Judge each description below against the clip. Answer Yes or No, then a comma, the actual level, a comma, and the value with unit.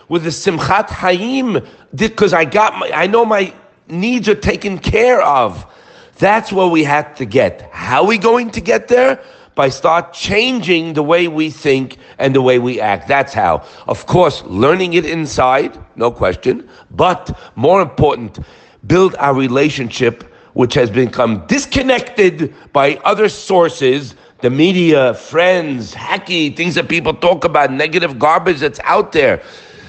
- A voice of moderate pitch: Yes, medium, 170 Hz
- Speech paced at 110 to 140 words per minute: No, average, 155 wpm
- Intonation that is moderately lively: No, wide, 6.6 semitones